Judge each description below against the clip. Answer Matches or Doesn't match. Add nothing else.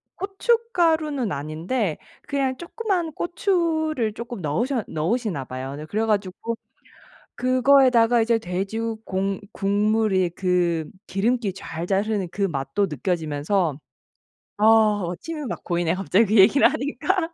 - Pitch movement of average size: Doesn't match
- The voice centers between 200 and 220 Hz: Matches